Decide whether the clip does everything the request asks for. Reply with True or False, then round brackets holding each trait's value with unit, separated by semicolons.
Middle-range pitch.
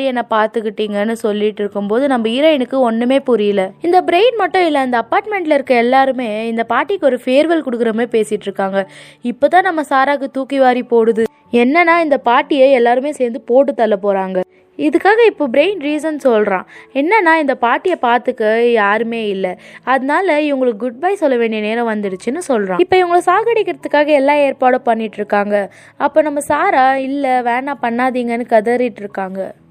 False (255 Hz)